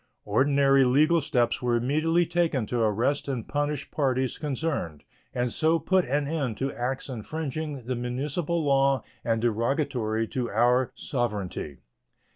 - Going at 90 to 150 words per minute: Yes, slow, 135 wpm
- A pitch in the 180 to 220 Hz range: No, low, 135 Hz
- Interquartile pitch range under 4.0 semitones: Yes, average, 3.6 semitones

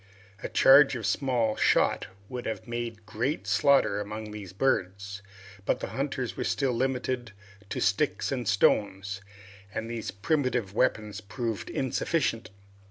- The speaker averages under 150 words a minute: Yes, average, 140 wpm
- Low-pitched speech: Yes, low, 115 Hz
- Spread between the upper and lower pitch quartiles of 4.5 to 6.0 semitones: No, average, 4.0 semitones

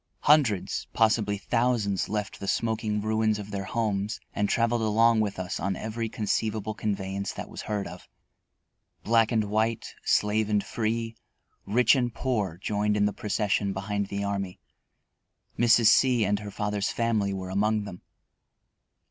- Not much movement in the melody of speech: Yes, narrow, 2.0 semitones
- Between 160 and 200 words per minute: No, average, 150 wpm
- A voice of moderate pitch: No, low, 105 Hz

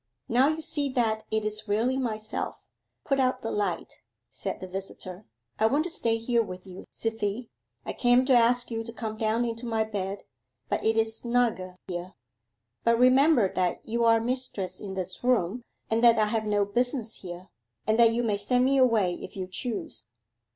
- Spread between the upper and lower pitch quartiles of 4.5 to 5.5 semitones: No, average, 3.2 semitones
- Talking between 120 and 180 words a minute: No, average, 190 wpm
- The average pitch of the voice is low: No, high, 225 Hz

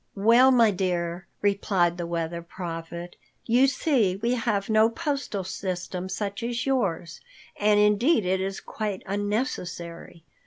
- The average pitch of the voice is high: Yes, high, 200 Hz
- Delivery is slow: Yes, slow, 130 wpm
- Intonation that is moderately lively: Yes, average, 4.5 semitones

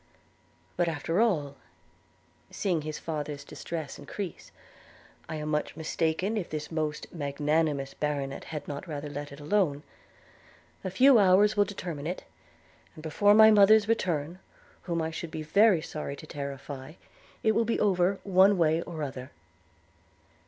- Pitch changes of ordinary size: Yes, average, 4.6 semitones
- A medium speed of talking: Yes, average, 150 wpm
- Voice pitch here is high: No, medium, 160 Hz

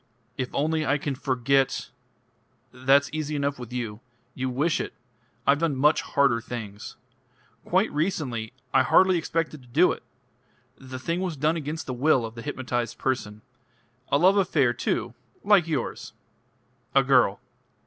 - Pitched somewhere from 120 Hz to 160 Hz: Yes, medium, 140 Hz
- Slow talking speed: No, average, 155 wpm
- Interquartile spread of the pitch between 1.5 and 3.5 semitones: No, average, 4.0 semitones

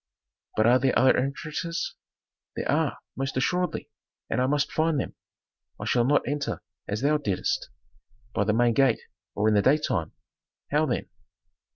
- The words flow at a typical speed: Yes, average, 160 wpm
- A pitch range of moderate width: Yes, average, 3.9 semitones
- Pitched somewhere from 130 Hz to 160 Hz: Yes, low, 135 Hz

